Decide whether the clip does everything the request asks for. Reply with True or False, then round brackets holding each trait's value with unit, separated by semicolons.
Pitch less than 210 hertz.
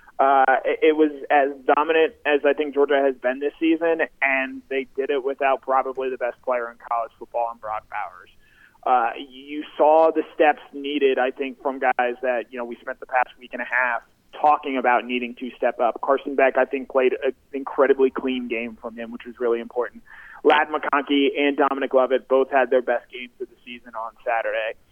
True (135 Hz)